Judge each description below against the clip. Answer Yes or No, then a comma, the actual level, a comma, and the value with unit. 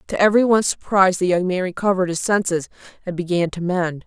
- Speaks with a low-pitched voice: No, medium, 185 Hz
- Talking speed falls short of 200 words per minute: Yes, average, 190 wpm